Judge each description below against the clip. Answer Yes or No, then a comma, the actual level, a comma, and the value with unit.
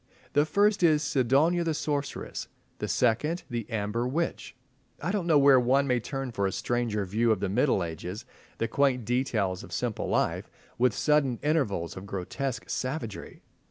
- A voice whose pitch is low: Yes, low, 125 Hz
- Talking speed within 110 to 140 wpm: No, average, 165 wpm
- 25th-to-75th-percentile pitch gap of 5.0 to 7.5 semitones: Yes, wide, 5.4 semitones